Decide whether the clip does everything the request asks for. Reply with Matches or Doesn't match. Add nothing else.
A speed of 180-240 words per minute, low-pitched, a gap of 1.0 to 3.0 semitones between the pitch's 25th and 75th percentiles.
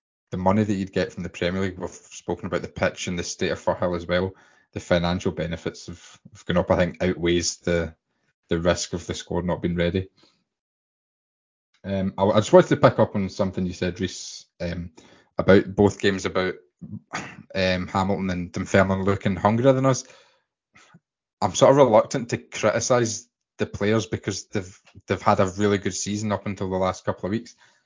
Matches